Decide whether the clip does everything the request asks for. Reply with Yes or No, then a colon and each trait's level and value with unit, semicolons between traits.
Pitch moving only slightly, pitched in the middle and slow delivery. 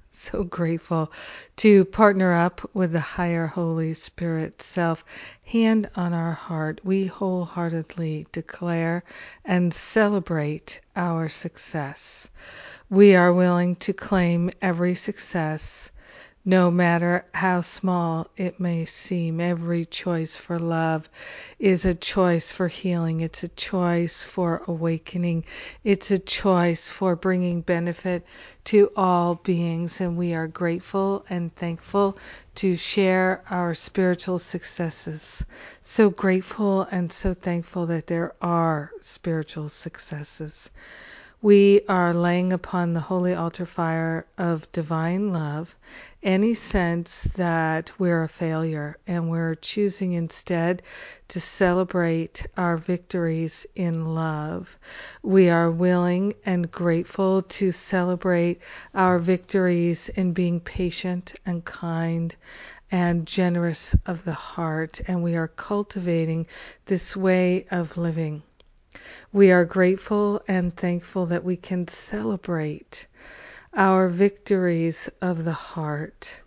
Yes: narrow, 2.0 semitones; medium, 175 Hz; slow, 115 wpm